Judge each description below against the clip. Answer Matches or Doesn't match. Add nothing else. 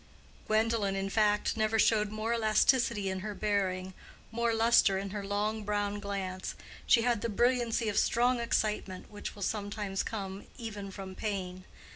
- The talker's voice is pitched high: Matches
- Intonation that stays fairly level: Matches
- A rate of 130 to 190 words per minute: Matches